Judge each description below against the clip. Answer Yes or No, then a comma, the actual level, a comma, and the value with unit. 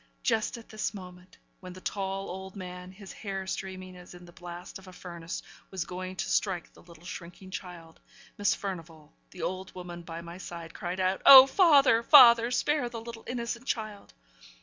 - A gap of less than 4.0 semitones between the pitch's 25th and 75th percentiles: Yes, average, 3.4 semitones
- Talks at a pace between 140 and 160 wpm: No, average, 185 wpm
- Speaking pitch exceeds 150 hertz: Yes, medium, 185 Hz